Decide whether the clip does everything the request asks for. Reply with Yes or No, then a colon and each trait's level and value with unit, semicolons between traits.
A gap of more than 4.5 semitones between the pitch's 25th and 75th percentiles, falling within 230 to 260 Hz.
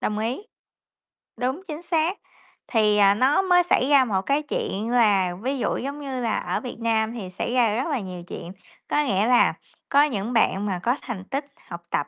Yes: average, 5.2 semitones; high, 240 Hz